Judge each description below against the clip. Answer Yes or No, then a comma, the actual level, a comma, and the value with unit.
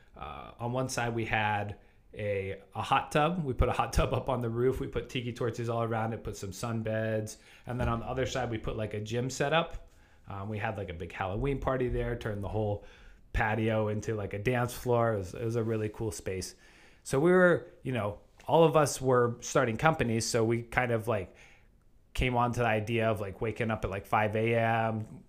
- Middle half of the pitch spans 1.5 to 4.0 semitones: Yes, average, 2.7 semitones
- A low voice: Yes, low, 115 Hz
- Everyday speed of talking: No, fast, 235 wpm